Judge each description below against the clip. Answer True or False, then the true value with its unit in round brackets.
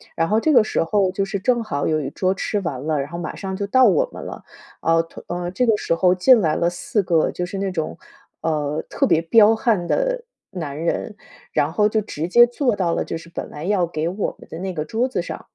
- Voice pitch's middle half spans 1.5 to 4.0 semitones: False (4.6 semitones)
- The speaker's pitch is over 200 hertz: False (185 Hz)